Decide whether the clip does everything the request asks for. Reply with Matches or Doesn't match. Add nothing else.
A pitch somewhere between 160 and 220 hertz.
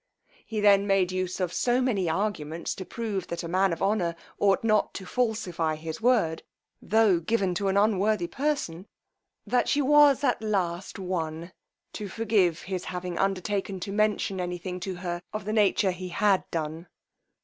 Matches